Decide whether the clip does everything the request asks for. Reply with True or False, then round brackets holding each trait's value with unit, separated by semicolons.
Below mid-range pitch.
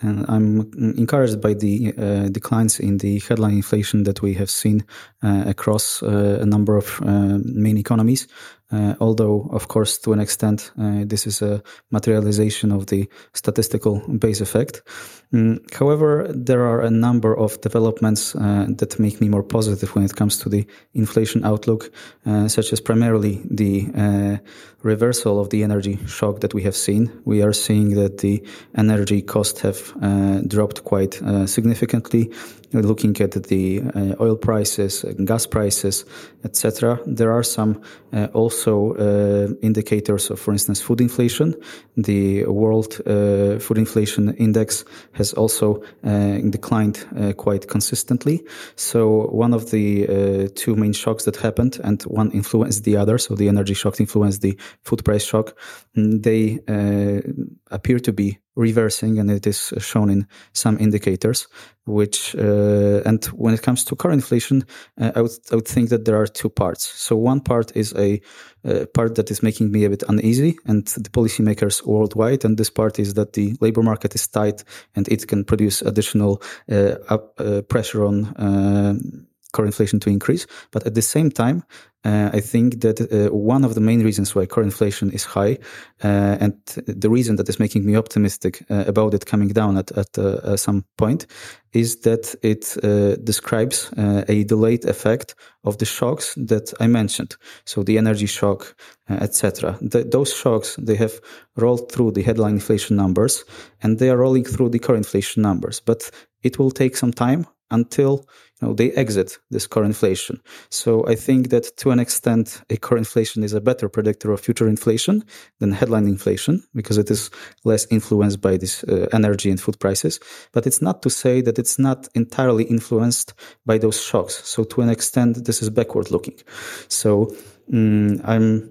True (110 Hz)